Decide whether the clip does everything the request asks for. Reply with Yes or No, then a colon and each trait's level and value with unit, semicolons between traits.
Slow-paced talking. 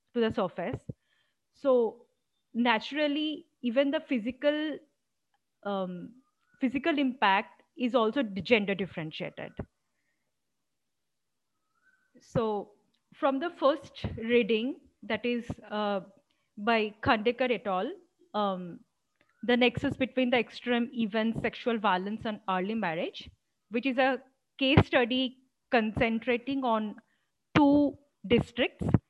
Yes: slow, 100 wpm